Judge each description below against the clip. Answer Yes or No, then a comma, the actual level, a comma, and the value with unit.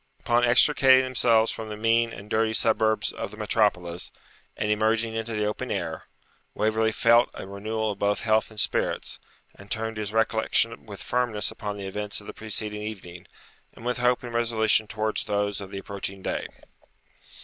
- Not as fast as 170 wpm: No, average, 175 wpm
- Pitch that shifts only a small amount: Yes, narrow, 1.7 semitones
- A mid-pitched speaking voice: No, low, 110 Hz